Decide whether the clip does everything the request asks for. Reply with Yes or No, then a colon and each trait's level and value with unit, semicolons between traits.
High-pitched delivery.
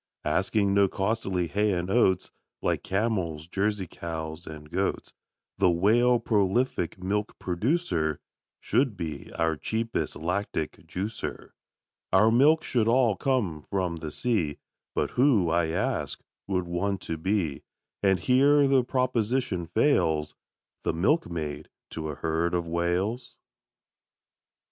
No: very low, 95 Hz